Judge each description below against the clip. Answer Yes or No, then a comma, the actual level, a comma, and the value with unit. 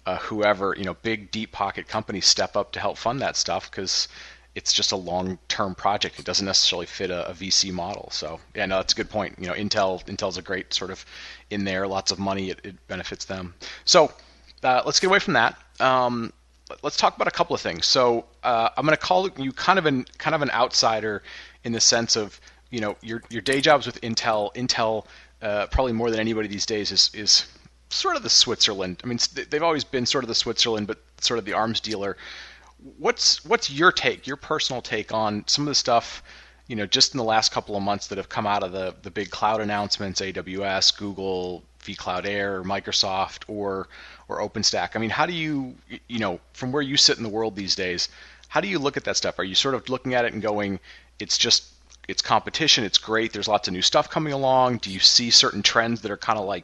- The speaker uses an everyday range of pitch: Yes, average, 3.9 semitones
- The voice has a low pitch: Yes, low, 105 Hz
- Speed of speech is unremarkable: No, fast, 230 wpm